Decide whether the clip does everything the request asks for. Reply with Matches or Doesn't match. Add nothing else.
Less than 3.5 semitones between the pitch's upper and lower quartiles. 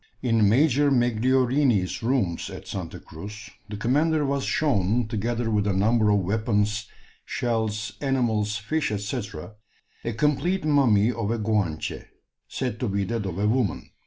Doesn't match